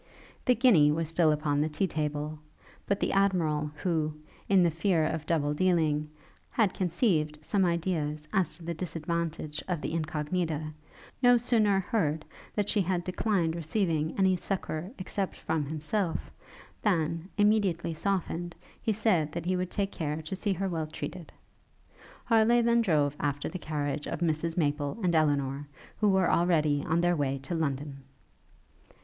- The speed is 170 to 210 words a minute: No, average, 155 wpm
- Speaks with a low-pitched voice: No, medium, 165 Hz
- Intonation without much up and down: No, average, 3.8 semitones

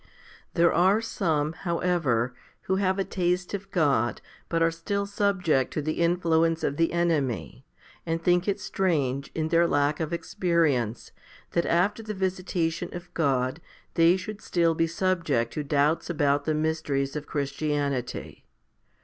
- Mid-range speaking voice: Yes, medium, 165 Hz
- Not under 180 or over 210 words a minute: No, average, 150 wpm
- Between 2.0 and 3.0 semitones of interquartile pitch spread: No, average, 3.6 semitones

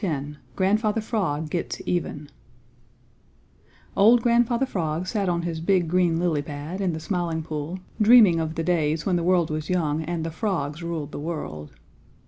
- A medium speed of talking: Yes, average, 165 wpm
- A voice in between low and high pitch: Yes, medium, 170 Hz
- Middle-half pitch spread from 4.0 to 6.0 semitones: No, average, 3.4 semitones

